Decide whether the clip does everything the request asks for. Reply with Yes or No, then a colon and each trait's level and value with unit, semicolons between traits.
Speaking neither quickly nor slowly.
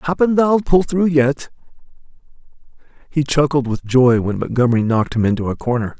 Yes: average, 160 wpm